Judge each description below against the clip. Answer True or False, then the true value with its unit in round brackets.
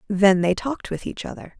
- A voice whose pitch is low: False (200 Hz)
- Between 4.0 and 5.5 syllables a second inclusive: False (5.8 syllables/s)